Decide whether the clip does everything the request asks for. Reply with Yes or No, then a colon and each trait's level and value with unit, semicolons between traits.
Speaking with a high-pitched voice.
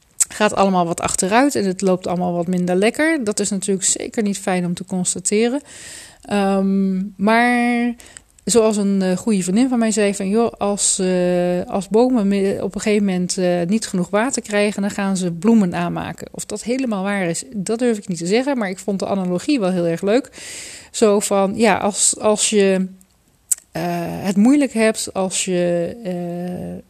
Yes: high, 200 Hz